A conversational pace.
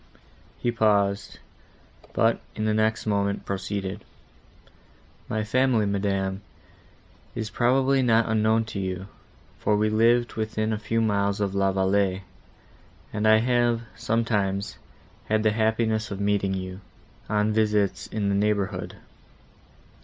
No: slow, 125 wpm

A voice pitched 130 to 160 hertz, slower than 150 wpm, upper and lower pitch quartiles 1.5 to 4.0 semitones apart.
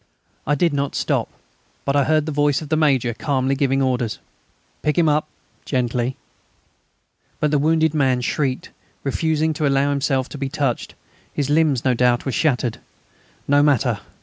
No: medium, 140 Hz; average, 165 wpm; narrow, 2.5 semitones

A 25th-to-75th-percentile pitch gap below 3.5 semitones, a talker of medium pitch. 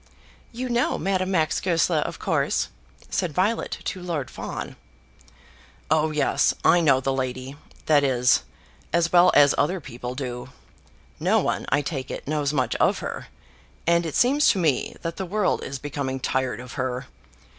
No: average, 5.0 semitones; medium, 150 Hz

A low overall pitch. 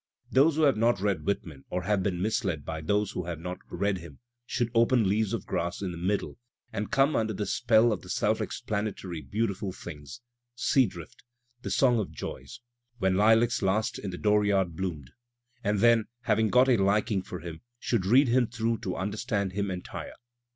Yes: low, 100 Hz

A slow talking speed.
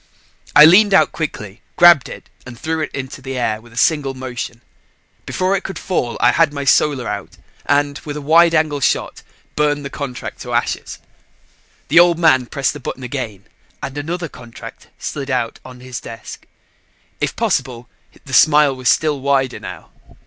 No: average, 175 wpm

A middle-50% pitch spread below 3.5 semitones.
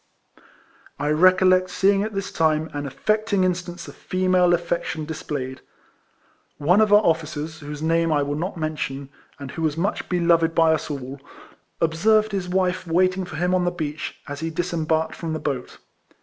Yes: average, 3.1 semitones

